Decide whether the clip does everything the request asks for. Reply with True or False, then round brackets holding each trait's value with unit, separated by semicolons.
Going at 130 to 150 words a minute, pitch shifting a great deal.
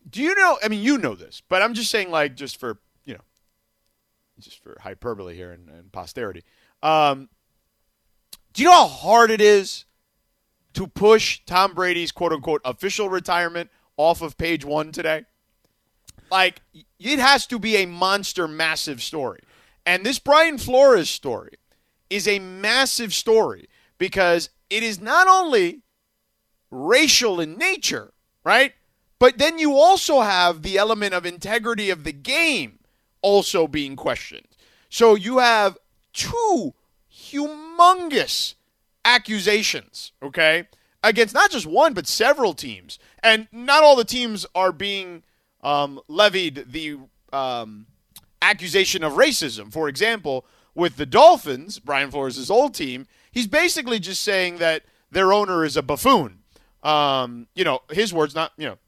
True (145 wpm; 7.6 semitones)